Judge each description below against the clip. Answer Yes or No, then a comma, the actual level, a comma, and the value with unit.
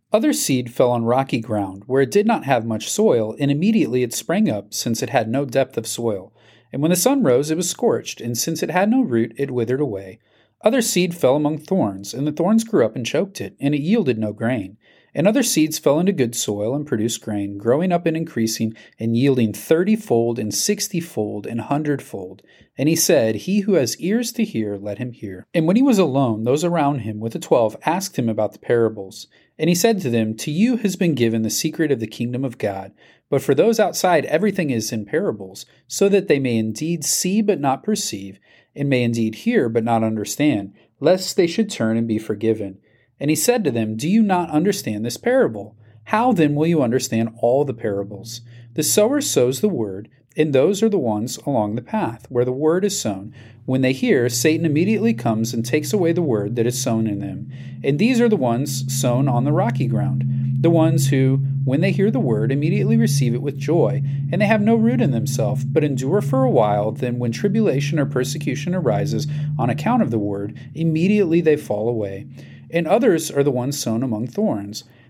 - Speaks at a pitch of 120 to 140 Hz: Yes, low, 135 Hz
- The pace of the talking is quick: Yes, fast, 215 wpm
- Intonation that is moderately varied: No, wide, 6.5 semitones